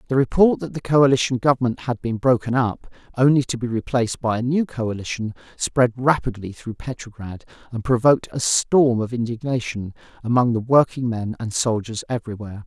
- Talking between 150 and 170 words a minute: Yes, average, 160 wpm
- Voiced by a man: Yes, male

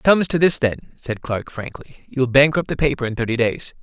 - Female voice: No, male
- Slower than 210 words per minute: No, fast, 250 wpm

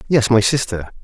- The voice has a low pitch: Yes, low, 115 Hz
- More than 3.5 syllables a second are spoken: Yes, 5.1 syllables/s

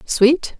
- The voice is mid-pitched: No, very high, 270 Hz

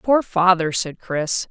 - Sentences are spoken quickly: No, average, 160 wpm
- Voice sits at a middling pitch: Yes, medium, 180 Hz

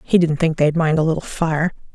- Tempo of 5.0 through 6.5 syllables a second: Yes, 5.4 syllables/s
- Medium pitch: Yes, medium, 160 Hz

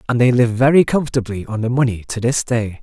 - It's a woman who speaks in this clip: No, male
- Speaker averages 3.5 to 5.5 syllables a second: No, 6.1 syllables/s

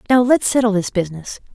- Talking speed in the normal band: Yes, average, 195 wpm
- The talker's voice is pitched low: No, high, 220 Hz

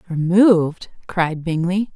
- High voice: No, medium, 175 Hz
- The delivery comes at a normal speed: No, slow, 90 wpm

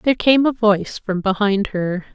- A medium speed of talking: Yes, average, 195 wpm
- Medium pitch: No, high, 210 Hz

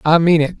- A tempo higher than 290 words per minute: Yes, fast, 300 wpm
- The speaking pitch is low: No, medium, 165 Hz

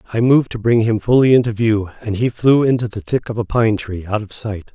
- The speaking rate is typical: No, fast, 265 wpm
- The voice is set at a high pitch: No, low, 110 Hz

